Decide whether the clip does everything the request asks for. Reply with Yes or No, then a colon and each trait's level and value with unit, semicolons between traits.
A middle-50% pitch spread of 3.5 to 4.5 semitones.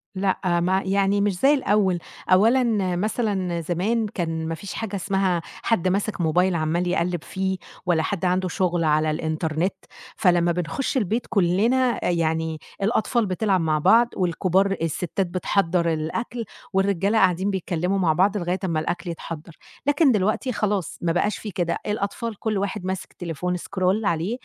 No: average, 3.1 semitones